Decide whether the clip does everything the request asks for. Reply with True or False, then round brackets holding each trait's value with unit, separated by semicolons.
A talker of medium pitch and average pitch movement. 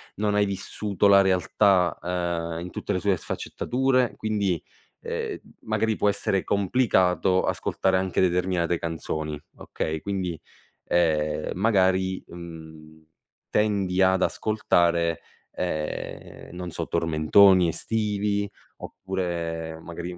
False (90 Hz; 3.1 semitones)